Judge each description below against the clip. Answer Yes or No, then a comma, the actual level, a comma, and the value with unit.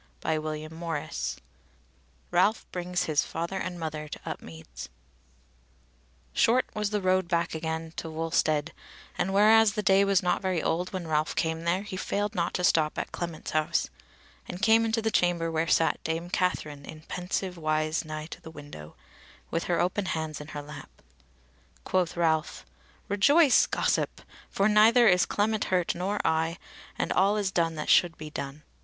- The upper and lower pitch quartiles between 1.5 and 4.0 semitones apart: Yes, average, 3.6 semitones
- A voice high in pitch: No, medium, 170 Hz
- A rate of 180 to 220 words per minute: No, average, 165 wpm